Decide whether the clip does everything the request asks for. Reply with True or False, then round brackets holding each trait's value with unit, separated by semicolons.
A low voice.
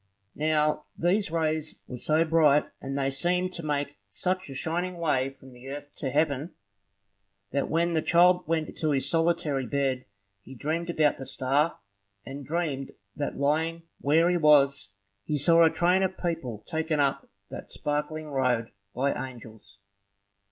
False (150 Hz)